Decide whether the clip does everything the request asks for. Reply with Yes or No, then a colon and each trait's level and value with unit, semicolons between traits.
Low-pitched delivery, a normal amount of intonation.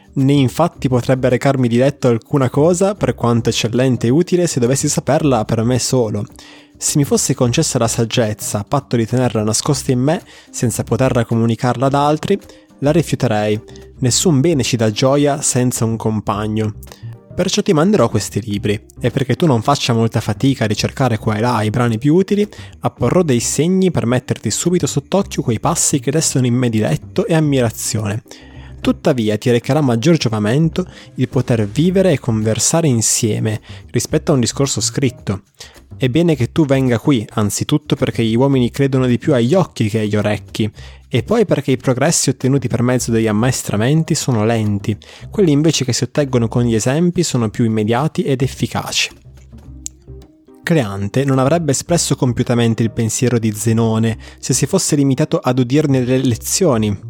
Yes: low, 125 Hz; average, 4.3 semitones